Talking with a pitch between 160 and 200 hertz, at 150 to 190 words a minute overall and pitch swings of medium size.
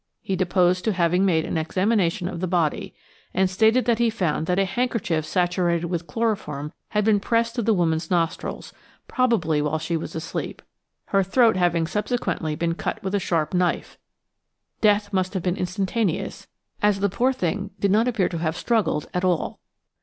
Yes: medium, 185 Hz; average, 180 wpm; average, 3.8 semitones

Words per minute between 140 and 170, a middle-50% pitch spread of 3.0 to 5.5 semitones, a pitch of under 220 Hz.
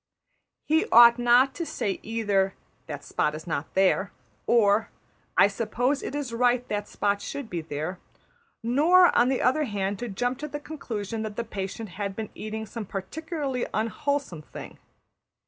No: average, 165 wpm; average, 4.5 semitones; high, 225 Hz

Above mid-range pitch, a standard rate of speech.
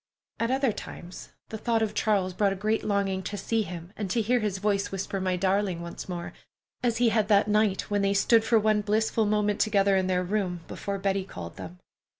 No: high, 200 Hz; fast, 215 wpm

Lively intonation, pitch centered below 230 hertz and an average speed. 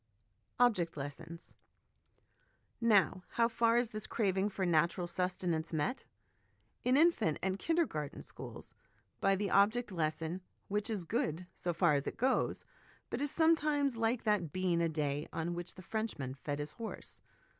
Yes: wide, 5.7 semitones; medium, 185 Hz; average, 155 wpm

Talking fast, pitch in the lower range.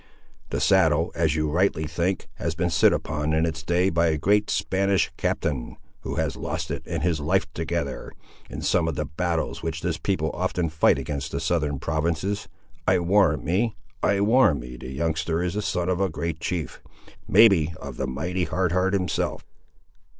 No: average, 185 wpm; very low, 85 Hz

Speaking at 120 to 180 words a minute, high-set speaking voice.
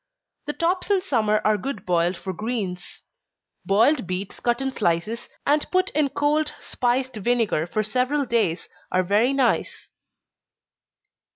Yes: slow, 135 wpm; high, 235 Hz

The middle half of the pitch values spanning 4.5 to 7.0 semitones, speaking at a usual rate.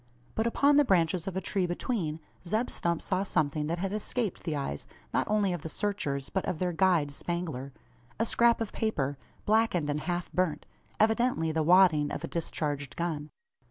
Yes: average, 5.2 semitones; average, 185 wpm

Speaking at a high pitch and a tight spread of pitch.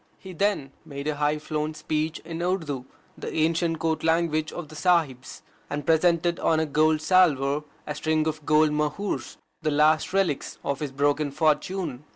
No: medium, 155 Hz; narrow, 1.8 semitones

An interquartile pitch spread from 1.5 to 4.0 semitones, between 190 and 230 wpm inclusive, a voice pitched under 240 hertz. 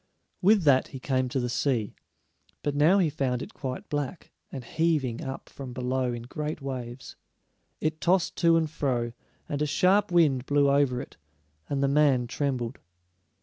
No: average, 3.2 semitones; average, 170 wpm; medium, 140 Hz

